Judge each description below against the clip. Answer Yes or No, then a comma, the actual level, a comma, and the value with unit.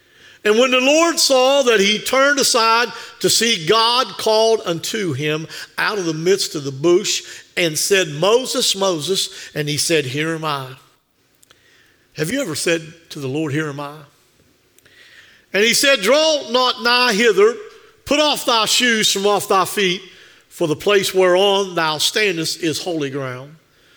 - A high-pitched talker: Yes, high, 195 Hz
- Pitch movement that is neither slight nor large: No, wide, 7.2 semitones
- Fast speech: No, average, 165 wpm